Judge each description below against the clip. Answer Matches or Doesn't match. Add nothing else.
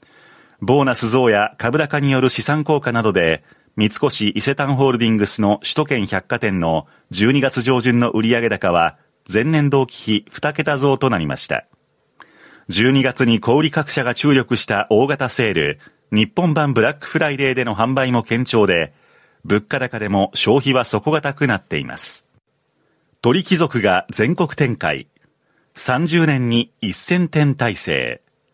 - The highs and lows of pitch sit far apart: Doesn't match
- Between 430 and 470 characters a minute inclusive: Doesn't match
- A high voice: Doesn't match